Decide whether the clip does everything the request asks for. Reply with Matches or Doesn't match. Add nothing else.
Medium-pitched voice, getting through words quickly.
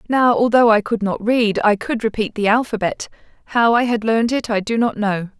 Doesn't match